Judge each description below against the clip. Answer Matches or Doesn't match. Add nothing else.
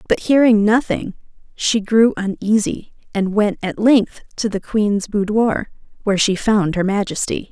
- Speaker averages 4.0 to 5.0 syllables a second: Matches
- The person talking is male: Doesn't match